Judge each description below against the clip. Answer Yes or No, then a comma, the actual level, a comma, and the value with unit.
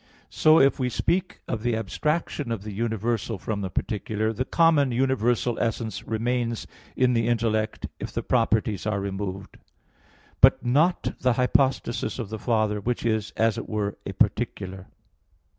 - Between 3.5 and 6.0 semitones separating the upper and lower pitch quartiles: No, average, 2.8 semitones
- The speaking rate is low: No, average, 155 wpm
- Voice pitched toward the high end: No, low, 115 Hz